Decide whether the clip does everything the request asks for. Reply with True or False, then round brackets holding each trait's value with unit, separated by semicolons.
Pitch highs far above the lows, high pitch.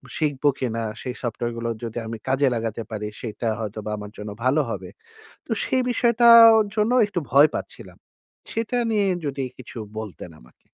False (6.1 semitones; 125 Hz)